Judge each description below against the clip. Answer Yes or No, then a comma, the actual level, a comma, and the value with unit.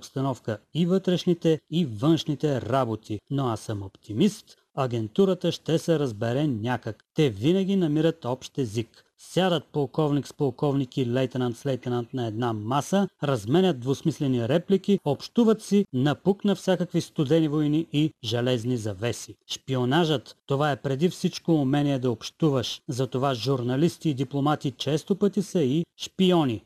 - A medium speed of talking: Yes, average, 130 wpm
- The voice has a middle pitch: Yes, medium, 145 Hz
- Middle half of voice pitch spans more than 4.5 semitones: Yes, average, 4.9 semitones